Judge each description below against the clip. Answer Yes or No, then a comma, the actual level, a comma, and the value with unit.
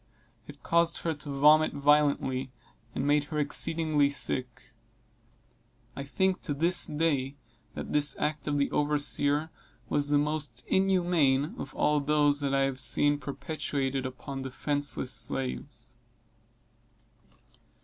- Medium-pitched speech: Yes, medium, 145 Hz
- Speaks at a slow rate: Yes, slow, 125 wpm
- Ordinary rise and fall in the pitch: No, narrow, 1.7 semitones